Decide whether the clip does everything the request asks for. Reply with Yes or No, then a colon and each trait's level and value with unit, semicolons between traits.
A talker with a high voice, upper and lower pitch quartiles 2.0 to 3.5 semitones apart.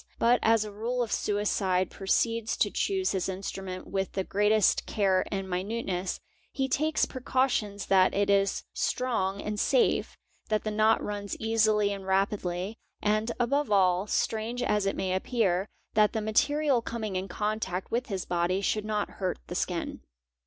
Yes: high, 210 Hz; average, 2.9 semitones